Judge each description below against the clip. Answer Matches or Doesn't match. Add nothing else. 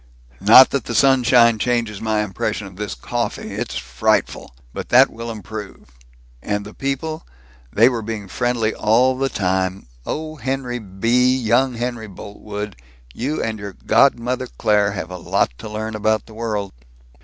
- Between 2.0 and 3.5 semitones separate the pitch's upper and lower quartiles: Matches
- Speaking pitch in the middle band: Doesn't match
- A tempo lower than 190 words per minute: Matches